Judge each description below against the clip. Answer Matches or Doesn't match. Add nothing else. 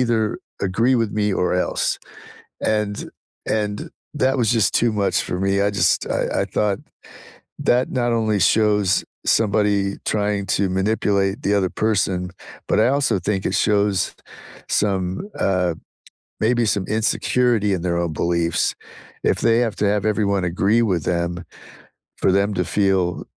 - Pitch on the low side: Matches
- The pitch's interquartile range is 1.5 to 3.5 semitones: Matches